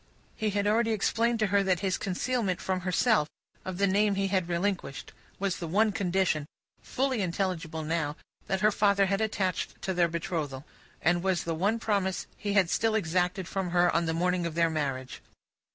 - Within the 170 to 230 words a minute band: Yes, average, 180 wpm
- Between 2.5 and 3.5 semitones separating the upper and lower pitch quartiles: Yes, average, 3.1 semitones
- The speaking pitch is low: No, medium, 185 Hz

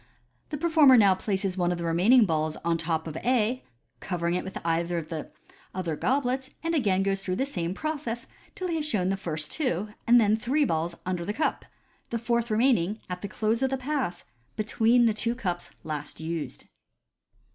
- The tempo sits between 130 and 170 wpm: No, average, 195 wpm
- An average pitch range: No, wide, 6.5 semitones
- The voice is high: Yes, high, 205 Hz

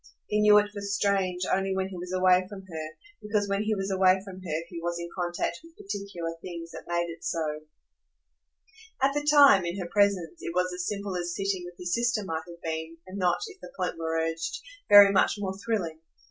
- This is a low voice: No, medium, 185 Hz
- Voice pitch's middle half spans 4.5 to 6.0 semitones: No, average, 2.8 semitones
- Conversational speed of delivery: No, fast, 215 wpm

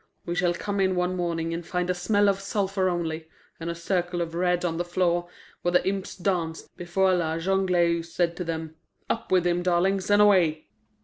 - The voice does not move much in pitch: Yes, narrow, 1.9 semitones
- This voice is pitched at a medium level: Yes, medium, 175 Hz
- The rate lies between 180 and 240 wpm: Yes, average, 200 wpm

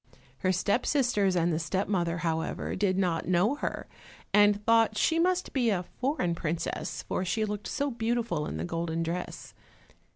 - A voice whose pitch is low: No, high, 195 Hz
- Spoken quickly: No, average, 170 wpm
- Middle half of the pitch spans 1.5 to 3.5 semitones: No, average, 5.0 semitones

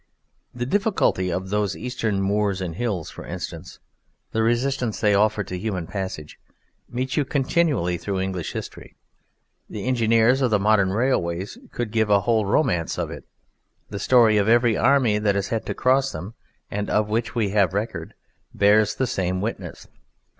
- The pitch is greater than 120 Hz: No, low, 105 Hz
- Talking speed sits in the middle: Yes, average, 170 wpm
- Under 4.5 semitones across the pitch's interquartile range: Yes, average, 3.6 semitones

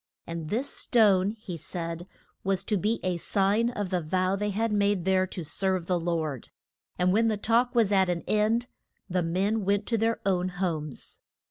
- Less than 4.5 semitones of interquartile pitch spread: Yes, average, 3.0 semitones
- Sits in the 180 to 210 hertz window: Yes, high, 190 Hz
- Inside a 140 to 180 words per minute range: No, average, 190 wpm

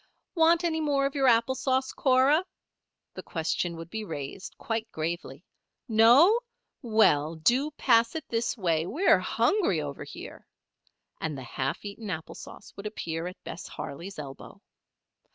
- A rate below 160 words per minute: Yes, average, 150 wpm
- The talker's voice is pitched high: Yes, high, 220 Hz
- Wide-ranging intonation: Yes, wide, 8.4 semitones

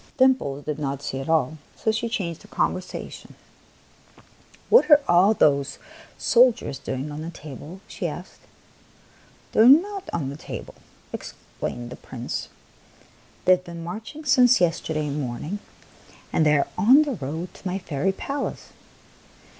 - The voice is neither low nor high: Yes, medium, 170 Hz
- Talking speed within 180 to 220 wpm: No, average, 160 wpm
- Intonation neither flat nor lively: No, wide, 7.8 semitones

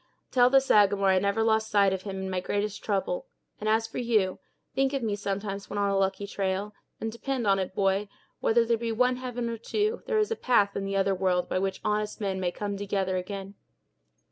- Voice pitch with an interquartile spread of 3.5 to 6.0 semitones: No, average, 3.0 semitones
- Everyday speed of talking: No, fast, 225 wpm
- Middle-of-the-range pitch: No, high, 205 Hz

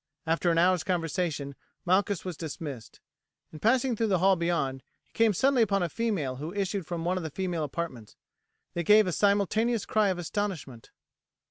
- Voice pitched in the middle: Yes, medium, 180 Hz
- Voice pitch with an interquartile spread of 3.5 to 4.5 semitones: Yes, average, 4.1 semitones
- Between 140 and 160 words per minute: No, average, 175 wpm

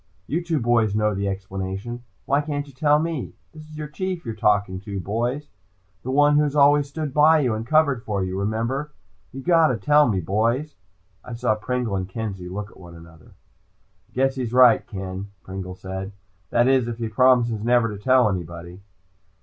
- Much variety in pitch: Yes, wide, 6.4 semitones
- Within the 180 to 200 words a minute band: Yes, average, 190 wpm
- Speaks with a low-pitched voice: Yes, low, 120 Hz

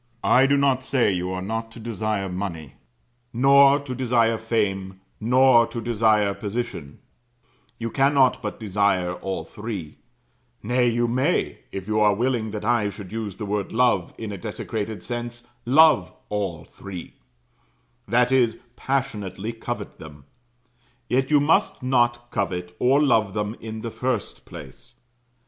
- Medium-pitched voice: No, low, 115 Hz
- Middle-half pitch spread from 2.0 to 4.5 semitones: Yes, average, 3.5 semitones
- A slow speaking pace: No, average, 145 wpm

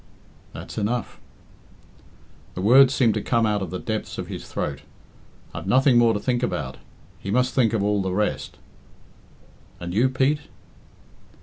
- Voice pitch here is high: No, low, 115 Hz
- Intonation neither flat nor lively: Yes, average, 3.7 semitones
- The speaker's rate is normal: Yes, average, 160 wpm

